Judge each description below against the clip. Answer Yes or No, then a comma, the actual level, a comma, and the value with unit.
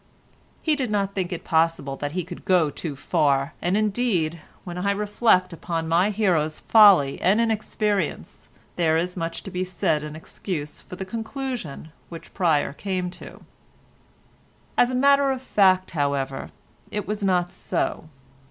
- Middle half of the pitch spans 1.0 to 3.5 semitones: No, average, 4.5 semitones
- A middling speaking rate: Yes, average, 155 wpm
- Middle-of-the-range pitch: Yes, medium, 180 Hz